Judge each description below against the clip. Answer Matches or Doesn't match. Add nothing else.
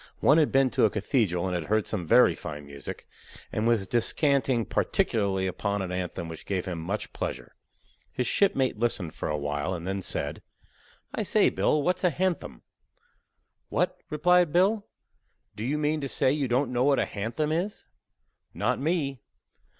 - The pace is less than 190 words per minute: Matches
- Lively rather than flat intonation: Matches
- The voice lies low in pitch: Matches